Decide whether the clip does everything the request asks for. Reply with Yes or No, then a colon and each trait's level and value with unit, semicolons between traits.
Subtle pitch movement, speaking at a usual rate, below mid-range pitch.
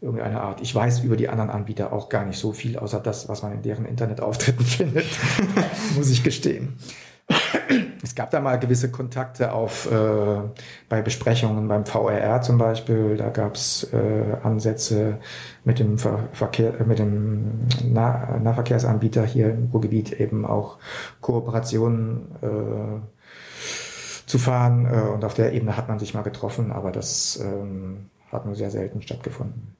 Yes: narrow, 2.3 semitones; average, 155 wpm; low, 115 Hz